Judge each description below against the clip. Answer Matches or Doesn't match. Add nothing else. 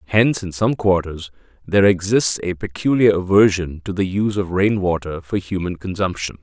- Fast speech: Doesn't match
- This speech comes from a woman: Doesn't match